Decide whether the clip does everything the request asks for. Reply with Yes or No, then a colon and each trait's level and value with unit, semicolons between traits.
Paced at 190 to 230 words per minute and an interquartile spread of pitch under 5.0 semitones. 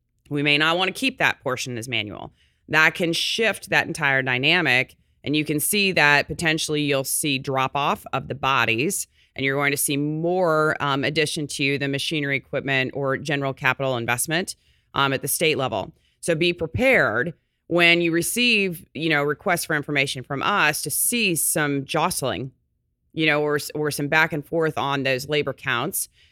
No: average, 180 wpm; average, 3.2 semitones